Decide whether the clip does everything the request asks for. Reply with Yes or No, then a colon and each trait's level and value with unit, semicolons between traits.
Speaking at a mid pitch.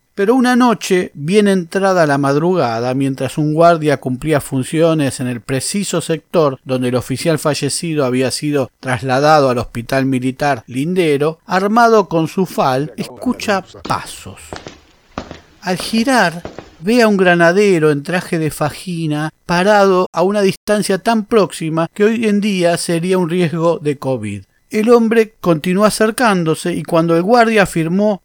Yes: medium, 165 Hz